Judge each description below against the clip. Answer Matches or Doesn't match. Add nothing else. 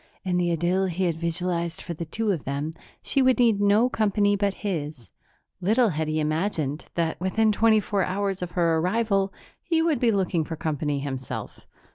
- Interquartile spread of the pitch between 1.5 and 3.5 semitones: Doesn't match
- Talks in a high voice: Doesn't match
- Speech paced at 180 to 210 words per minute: Matches